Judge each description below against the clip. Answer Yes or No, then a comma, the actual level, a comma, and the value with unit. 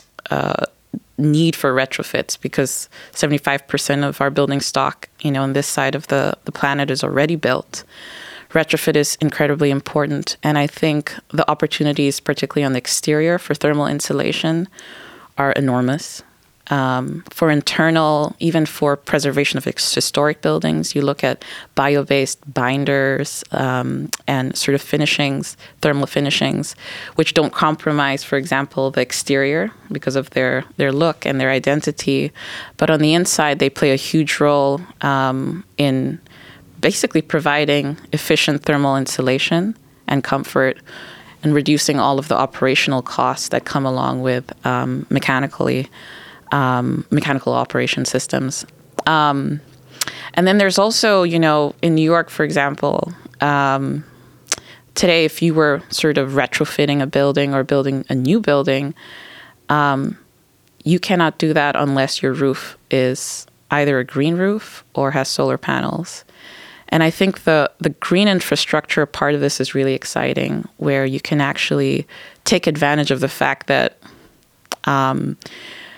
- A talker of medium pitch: Yes, medium, 145 Hz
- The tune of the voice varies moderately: No, narrow, 2.2 semitones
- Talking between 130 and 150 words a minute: Yes, average, 140 wpm